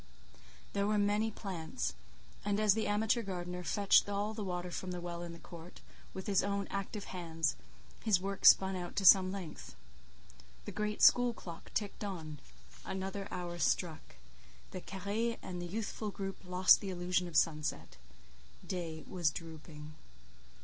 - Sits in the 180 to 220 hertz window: Yes, medium, 185 Hz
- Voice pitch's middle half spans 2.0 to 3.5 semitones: Yes, average, 2.7 semitones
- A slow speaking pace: No, average, 155 wpm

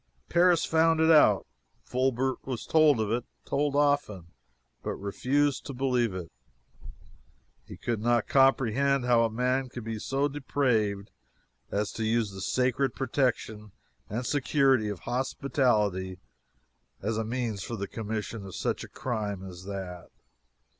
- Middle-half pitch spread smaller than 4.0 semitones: No, average, 4.3 semitones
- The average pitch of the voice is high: No, low, 120 Hz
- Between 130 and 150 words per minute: Yes, average, 140 wpm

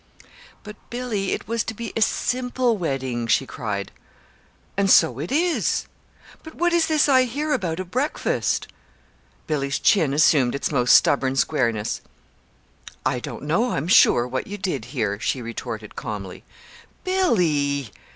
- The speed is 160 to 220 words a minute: No, average, 145 wpm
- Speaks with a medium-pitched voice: Yes, medium, 160 Hz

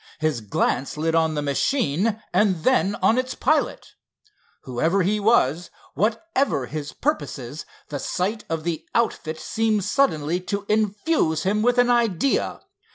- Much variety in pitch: Yes, wide, 6.3 semitones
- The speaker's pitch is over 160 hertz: Yes, high, 190 Hz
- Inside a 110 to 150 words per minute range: Yes, average, 140 wpm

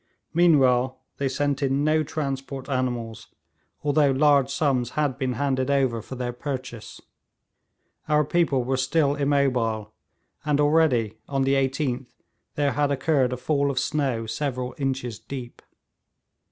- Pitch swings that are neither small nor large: No, narrow, 2.2 semitones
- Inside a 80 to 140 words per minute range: Yes, slow, 135 wpm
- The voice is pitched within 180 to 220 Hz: No, low, 135 Hz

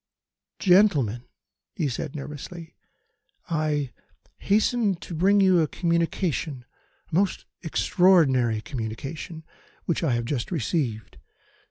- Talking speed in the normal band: No, slow, 105 wpm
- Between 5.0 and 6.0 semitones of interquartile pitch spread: Yes, wide, 5.4 semitones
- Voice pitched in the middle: Yes, medium, 160 Hz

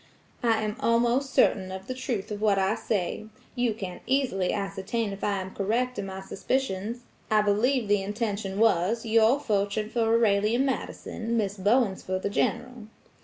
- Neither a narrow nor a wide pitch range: Yes, average, 3.1 semitones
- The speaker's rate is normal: Yes, average, 170 wpm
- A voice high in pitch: Yes, high, 215 Hz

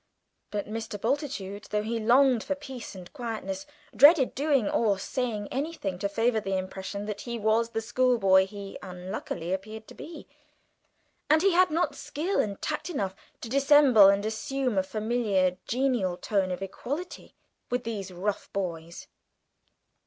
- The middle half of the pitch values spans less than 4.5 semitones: No, wide, 5.4 semitones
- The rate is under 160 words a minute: Yes, average, 150 wpm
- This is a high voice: Yes, high, 220 Hz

